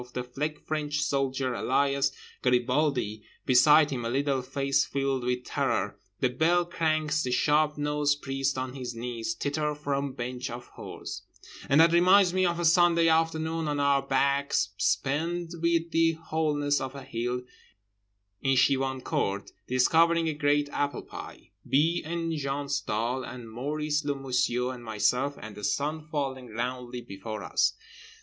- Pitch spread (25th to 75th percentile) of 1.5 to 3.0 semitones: No, average, 3.6 semitones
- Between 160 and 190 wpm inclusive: No, average, 150 wpm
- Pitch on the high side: No, medium, 140 Hz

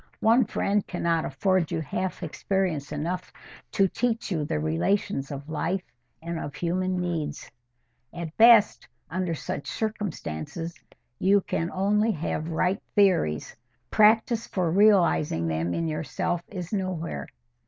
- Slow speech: Yes, slow, 130 wpm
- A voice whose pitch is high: No, medium, 175 Hz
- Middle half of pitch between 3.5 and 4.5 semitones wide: Yes, average, 4.2 semitones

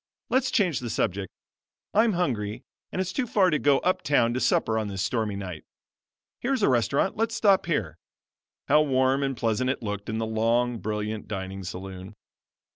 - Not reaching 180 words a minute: No, average, 185 wpm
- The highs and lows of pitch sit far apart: Yes, wide, 6.7 semitones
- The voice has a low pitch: Yes, low, 115 Hz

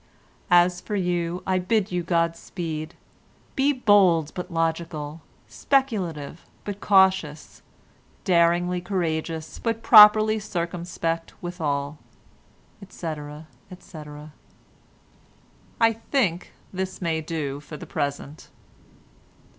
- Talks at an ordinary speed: No, slow, 95 wpm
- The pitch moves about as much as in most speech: Yes, average, 3.2 semitones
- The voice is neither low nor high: Yes, medium, 175 Hz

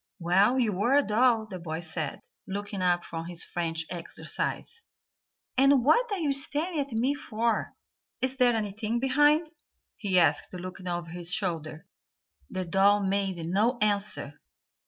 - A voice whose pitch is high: Yes, high, 205 Hz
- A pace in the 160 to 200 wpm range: No, average, 150 wpm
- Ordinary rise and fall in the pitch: No, wide, 6.4 semitones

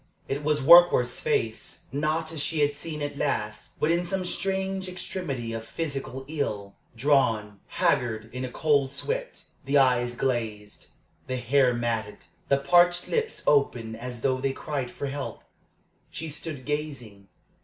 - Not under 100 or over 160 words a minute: Yes, average, 150 wpm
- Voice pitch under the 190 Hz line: Yes, medium, 140 Hz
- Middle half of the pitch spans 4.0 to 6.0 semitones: Yes, average, 4.7 semitones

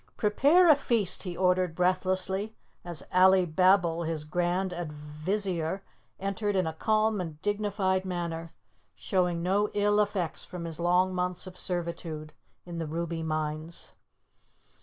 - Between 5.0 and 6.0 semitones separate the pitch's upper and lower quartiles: No, average, 2.8 semitones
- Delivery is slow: Yes, slow, 130 wpm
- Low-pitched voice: No, medium, 180 Hz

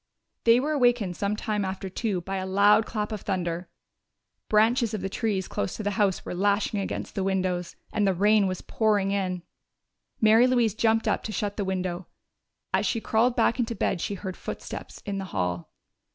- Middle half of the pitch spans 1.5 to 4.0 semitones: Yes, average, 2.7 semitones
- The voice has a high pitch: Yes, high, 200 Hz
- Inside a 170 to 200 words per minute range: Yes, average, 190 wpm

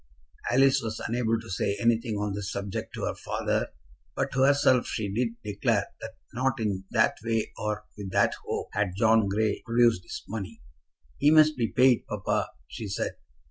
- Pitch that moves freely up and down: No, average, 2.9 semitones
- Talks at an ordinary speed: Yes, average, 180 wpm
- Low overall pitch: Yes, low, 110 Hz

